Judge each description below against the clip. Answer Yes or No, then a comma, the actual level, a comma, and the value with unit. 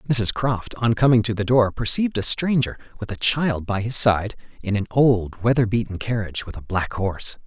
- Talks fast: Yes, fast, 210 wpm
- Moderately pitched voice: No, low, 110 Hz